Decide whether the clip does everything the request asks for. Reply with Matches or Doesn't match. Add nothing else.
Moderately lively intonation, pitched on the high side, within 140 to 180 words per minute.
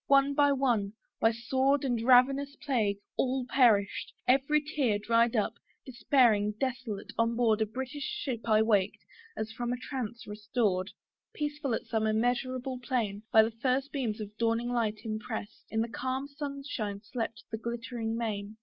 Matches